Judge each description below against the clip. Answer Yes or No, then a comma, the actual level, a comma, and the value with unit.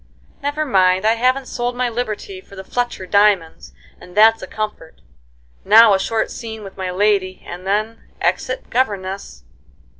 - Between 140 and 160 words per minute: Yes, average, 155 wpm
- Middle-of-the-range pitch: No, high, 210 Hz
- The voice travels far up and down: No, average, 3.5 semitones